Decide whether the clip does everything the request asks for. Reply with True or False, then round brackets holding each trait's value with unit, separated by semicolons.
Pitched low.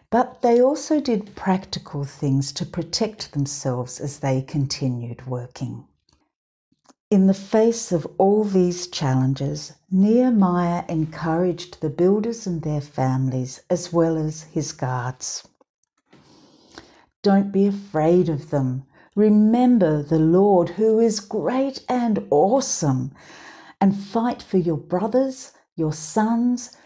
False (175 Hz)